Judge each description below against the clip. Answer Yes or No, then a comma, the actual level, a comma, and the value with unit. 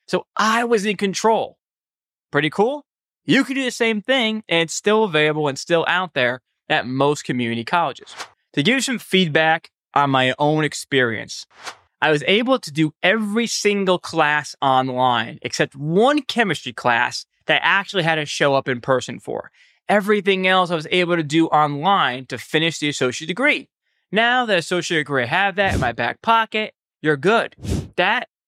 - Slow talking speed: No, average, 175 wpm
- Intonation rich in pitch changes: Yes, wide, 6.4 semitones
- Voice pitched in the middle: Yes, medium, 170 Hz